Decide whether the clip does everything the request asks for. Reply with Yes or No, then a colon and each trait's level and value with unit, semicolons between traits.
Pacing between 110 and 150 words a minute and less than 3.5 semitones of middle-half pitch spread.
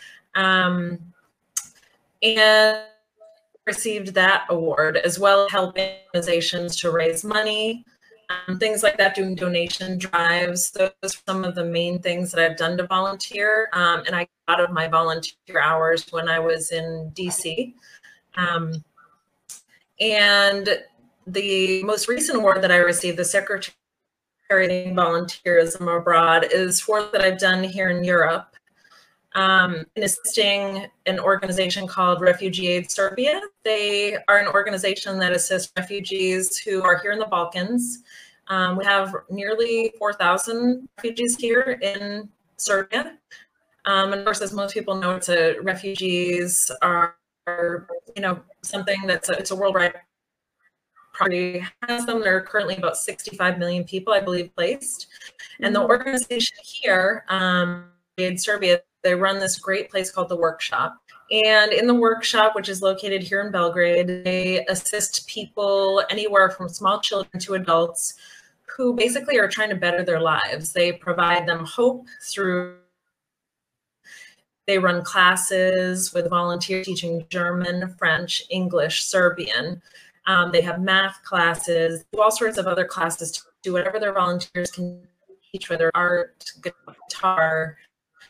Yes: average, 140 wpm; narrow, 2.6 semitones